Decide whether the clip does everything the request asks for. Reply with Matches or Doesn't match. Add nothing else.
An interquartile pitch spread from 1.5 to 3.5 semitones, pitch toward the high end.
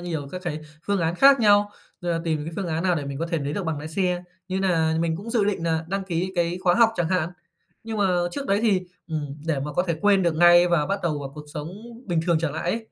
Doesn't match